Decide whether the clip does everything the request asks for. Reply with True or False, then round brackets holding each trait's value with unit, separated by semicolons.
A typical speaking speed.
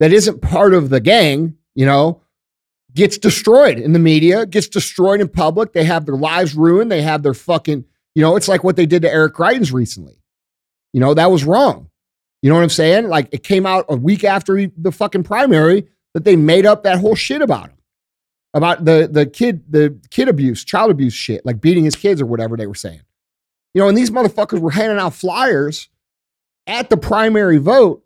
False (210 wpm)